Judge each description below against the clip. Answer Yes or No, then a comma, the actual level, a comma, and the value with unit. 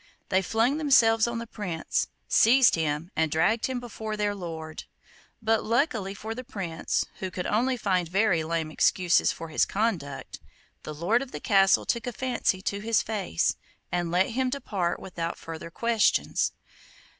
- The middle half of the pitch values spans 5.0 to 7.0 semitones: Yes, wide, 5.4 semitones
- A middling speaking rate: Yes, average, 165 wpm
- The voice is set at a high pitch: Yes, high, 205 Hz